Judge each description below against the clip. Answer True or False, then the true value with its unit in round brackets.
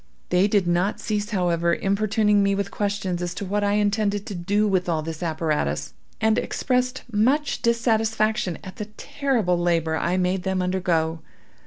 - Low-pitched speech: False (195 Hz)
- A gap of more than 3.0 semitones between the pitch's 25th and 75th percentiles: True (3.4 semitones)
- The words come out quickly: False (165 wpm)